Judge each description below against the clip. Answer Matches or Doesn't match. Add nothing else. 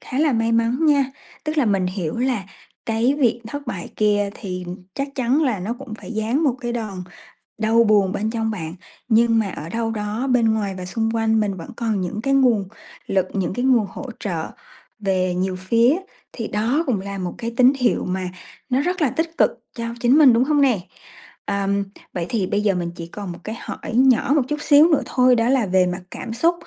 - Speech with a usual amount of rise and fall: Matches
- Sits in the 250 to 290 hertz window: Doesn't match